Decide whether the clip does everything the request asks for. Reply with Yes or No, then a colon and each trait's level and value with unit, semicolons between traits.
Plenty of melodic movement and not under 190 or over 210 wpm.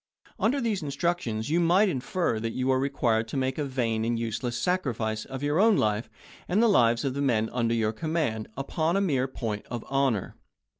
Yes: wide, 6.3 semitones; average, 200 wpm